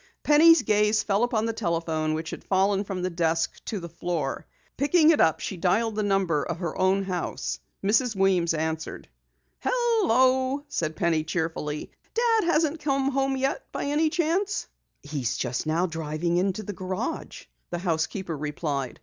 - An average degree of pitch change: No, wide, 8.5 semitones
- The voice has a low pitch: No, high, 190 Hz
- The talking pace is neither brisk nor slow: Yes, average, 160 wpm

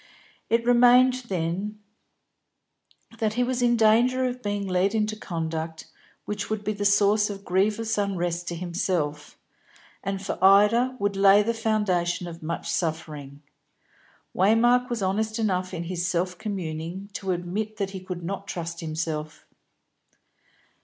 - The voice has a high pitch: Yes, high, 195 Hz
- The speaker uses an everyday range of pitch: Yes, average, 3.8 semitones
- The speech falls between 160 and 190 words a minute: No, average, 140 wpm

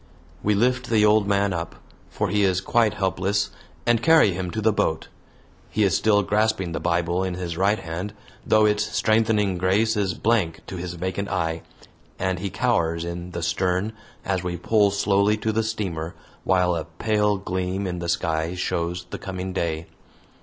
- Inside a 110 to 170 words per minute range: No, average, 180 wpm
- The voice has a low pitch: Yes, very low, 95 Hz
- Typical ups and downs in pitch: Yes, average, 3.3 semitones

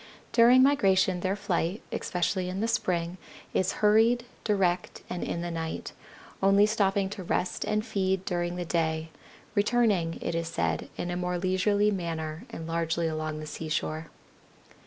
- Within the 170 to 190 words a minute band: No, average, 155 wpm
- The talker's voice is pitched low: No, medium, 180 Hz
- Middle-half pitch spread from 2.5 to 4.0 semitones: Yes, average, 3.5 semitones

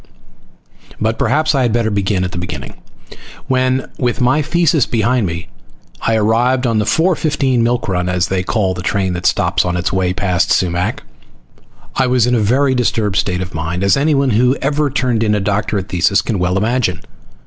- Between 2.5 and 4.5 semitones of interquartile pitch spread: No, wide, 5.6 semitones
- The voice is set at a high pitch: No, low, 110 Hz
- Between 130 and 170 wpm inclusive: No, average, 190 wpm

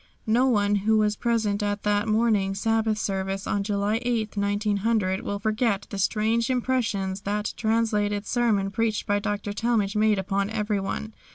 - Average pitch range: No, narrow, 1.7 semitones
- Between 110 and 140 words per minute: No, average, 155 wpm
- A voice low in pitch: No, high, 210 Hz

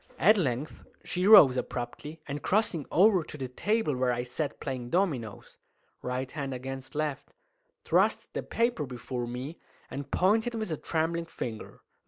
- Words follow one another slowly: No, average, 155 wpm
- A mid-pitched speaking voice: Yes, medium, 145 Hz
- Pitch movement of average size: No, wide, 5.7 semitones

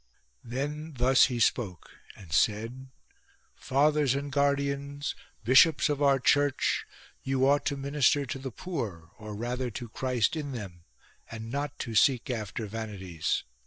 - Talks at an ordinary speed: Yes, average, 150 wpm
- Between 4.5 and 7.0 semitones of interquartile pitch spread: No, average, 4.1 semitones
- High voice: No, low, 130 Hz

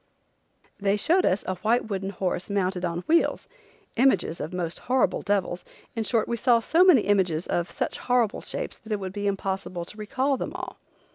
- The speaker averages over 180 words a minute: Yes, average, 190 wpm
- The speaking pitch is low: No, high, 200 Hz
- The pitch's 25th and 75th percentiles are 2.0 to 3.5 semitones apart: No, average, 4.4 semitones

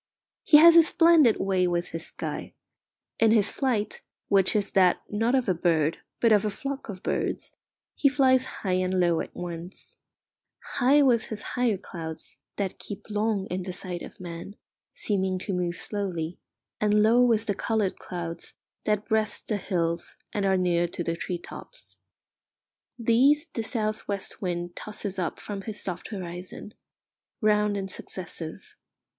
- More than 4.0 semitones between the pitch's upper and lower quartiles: No, average, 3.7 semitones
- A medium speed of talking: Yes, average, 160 wpm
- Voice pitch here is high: Yes, high, 200 Hz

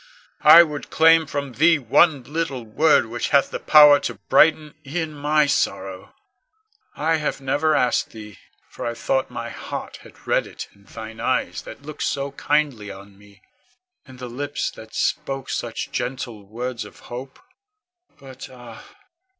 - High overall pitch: No, low, 135 Hz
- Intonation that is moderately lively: Yes, average, 4.6 semitones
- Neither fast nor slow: Yes, average, 160 wpm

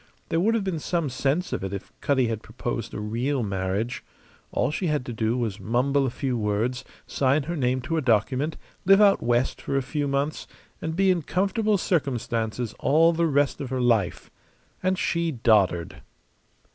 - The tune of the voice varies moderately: No, wide, 5.8 semitones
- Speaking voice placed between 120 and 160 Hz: Yes, low, 135 Hz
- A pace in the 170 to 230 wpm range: Yes, average, 185 wpm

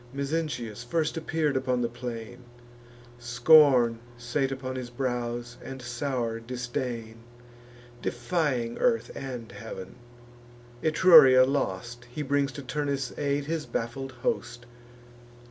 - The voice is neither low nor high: No, low, 125 Hz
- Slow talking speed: Yes, slow, 110 wpm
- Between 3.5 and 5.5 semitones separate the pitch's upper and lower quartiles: No, average, 2.9 semitones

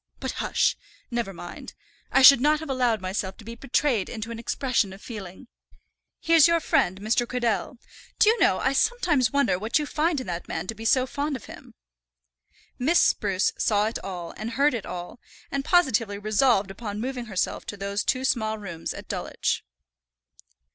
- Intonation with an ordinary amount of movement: Yes, average, 5.0 semitones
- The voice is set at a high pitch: Yes, high, 230 Hz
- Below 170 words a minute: No, average, 180 wpm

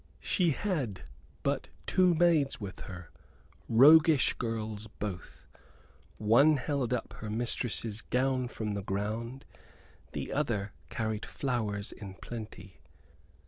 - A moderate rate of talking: No, slow, 110 wpm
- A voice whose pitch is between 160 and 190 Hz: No, low, 115 Hz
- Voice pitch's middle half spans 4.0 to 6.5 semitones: Yes, average, 4.5 semitones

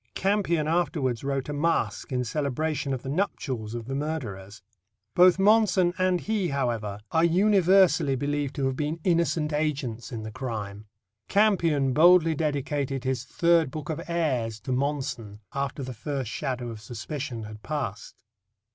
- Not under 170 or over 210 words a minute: No, average, 150 wpm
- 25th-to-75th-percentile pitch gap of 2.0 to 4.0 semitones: No, average, 5.0 semitones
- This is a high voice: No, medium, 140 Hz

